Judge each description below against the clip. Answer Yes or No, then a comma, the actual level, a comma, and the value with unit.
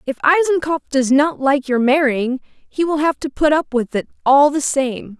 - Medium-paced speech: No, fast, 210 wpm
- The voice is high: Yes, very high, 280 Hz